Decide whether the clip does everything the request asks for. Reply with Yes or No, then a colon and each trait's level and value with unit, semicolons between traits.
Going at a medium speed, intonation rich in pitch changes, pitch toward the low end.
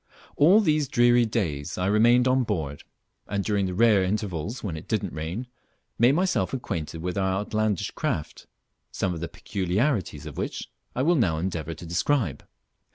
Yes: average, 165 wpm; wide, 6.1 semitones; low, 100 Hz